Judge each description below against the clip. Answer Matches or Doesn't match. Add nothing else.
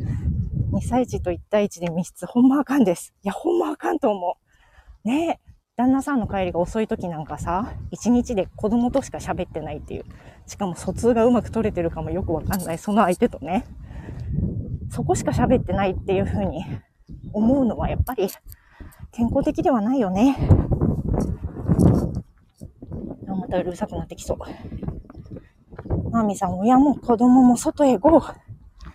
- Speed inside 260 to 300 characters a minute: Doesn't match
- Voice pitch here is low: Doesn't match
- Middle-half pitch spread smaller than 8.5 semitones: Matches